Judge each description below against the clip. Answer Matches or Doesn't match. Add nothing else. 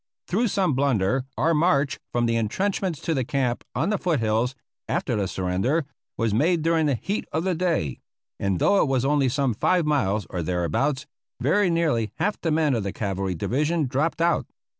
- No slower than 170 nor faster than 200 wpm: Matches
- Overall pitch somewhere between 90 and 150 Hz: Matches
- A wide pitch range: Matches